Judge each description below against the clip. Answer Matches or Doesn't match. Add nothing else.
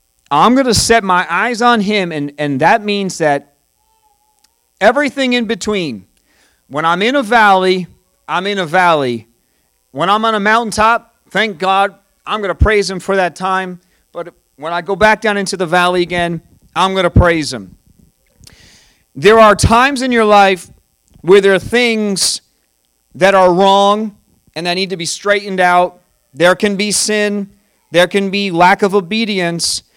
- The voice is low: Doesn't match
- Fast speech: Doesn't match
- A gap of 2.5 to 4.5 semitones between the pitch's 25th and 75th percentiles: Matches